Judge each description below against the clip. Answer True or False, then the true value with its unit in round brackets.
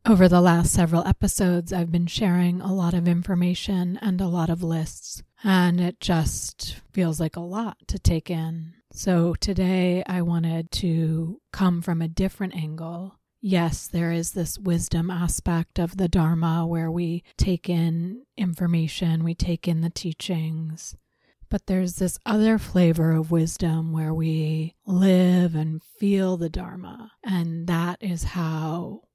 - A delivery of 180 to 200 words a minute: False (150 wpm)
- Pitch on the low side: False (175 Hz)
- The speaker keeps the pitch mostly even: True (1.9 semitones)